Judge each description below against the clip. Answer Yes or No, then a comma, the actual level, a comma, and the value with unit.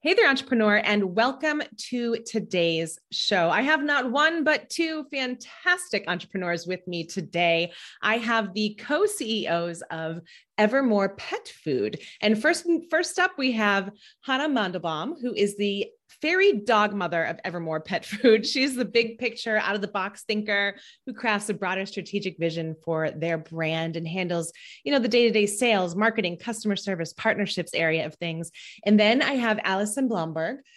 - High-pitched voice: Yes, high, 210 Hz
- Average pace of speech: Yes, average, 165 wpm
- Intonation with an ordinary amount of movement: No, wide, 6.2 semitones